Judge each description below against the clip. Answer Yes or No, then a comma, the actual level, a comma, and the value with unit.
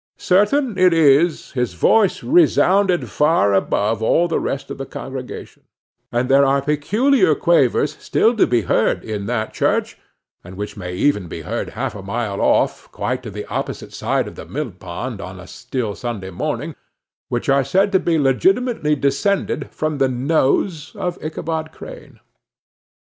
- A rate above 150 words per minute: Yes, average, 160 wpm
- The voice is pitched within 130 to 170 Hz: Yes, medium, 140 Hz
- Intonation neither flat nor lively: No, wide, 7.3 semitones